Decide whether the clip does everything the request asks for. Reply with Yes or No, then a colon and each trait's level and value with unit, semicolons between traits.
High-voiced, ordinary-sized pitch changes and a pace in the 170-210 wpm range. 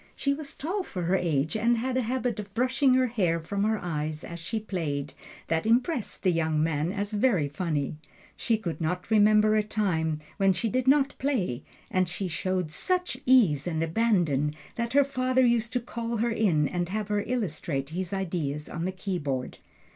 No: high, 195 Hz; wide, 6.3 semitones; average, 190 wpm